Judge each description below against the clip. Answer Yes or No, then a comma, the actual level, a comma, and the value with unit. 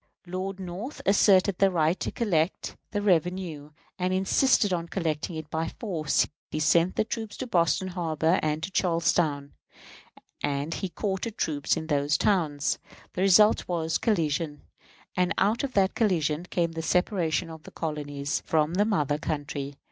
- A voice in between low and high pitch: Yes, medium, 170 Hz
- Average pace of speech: Yes, average, 155 wpm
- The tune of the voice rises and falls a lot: No, average, 3.7 semitones